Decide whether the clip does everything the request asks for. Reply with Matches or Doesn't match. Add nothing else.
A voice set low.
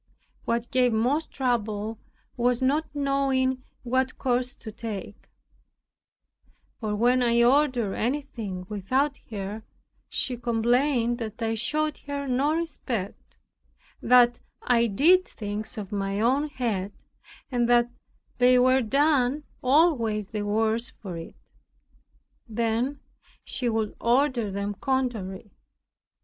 Doesn't match